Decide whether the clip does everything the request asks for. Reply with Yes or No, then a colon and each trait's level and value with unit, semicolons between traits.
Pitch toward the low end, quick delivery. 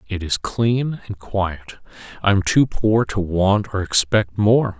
No: low, 105 Hz; average, 175 wpm